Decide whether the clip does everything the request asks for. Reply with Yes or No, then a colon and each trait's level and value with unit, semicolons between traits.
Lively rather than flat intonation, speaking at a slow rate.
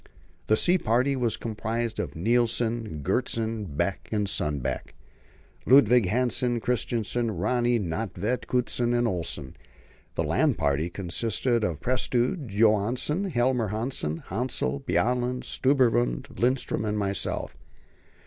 No: average, 3.8 semitones; slow, 110 wpm